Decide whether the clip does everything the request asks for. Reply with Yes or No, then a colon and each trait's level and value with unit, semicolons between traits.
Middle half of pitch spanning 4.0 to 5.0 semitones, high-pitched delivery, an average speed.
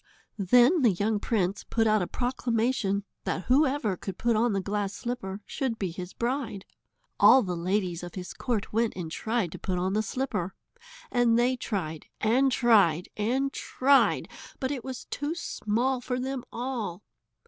Yes: average, 4.7 semitones; high, 225 Hz; average, 170 wpm